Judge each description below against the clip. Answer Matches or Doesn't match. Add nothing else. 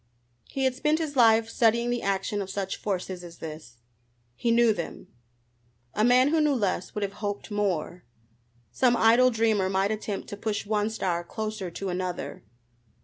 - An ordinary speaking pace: Matches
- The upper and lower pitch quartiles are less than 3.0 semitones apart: Doesn't match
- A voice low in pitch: Doesn't match